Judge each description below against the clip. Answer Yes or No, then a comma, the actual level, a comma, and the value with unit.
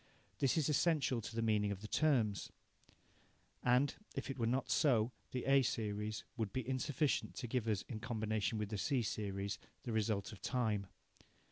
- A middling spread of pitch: Yes, average, 3.6 semitones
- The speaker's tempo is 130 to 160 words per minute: No, average, 175 wpm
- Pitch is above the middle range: No, low, 115 Hz